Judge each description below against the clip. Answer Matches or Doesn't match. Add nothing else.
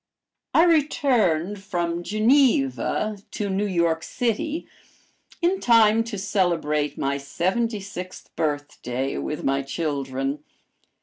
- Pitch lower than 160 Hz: Doesn't match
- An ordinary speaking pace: Doesn't match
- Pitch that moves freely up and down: Matches